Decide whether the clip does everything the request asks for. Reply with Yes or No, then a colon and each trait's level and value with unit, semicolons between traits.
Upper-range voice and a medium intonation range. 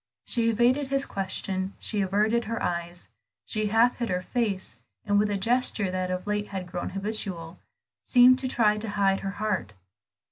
Yes: high, 205 Hz; average, 3.4 semitones